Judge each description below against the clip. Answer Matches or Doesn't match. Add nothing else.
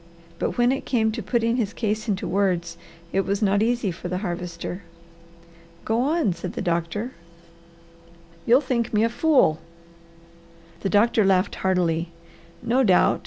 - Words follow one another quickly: Doesn't match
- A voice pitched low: Doesn't match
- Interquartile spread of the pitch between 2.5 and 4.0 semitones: Doesn't match